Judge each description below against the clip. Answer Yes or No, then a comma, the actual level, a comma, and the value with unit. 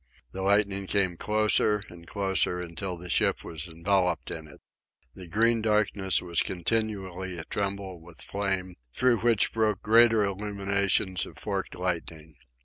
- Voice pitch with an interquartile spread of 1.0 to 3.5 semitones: Yes, average, 2.8 semitones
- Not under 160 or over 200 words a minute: No, average, 140 wpm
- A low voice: Yes, very low, 95 Hz